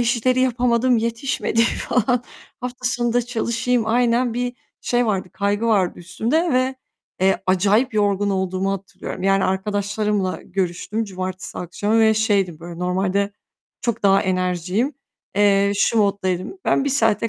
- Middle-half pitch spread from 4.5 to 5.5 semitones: No, average, 3.9 semitones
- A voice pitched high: Yes, high, 210 Hz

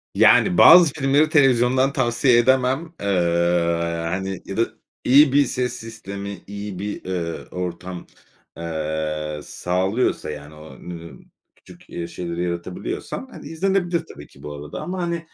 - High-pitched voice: No, very low, 95 Hz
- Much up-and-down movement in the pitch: Yes, wide, 7.8 semitones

